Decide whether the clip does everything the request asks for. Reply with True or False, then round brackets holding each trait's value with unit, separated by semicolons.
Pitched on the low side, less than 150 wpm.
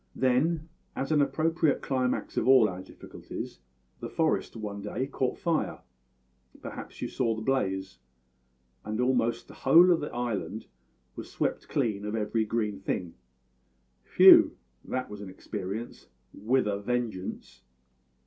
True (115 Hz; 140 wpm)